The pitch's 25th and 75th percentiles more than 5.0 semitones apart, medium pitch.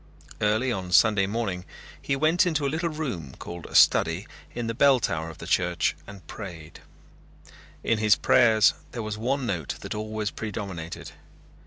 No: wide, 5.5 semitones; low, 110 Hz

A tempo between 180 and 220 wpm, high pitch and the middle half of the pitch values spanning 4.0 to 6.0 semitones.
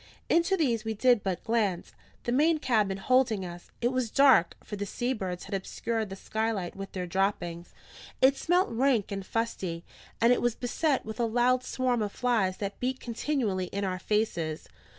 Yes: average, 185 wpm; high, 220 Hz; average, 4.5 semitones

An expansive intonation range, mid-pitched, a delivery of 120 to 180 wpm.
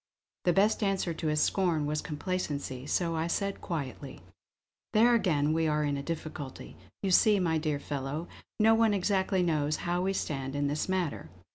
No: average, 4.3 semitones; medium, 165 Hz; average, 175 wpm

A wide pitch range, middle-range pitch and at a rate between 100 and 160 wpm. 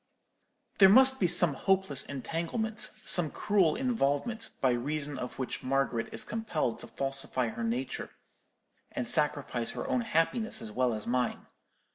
Yes: wide, 7.2 semitones; medium, 145 Hz; average, 145 wpm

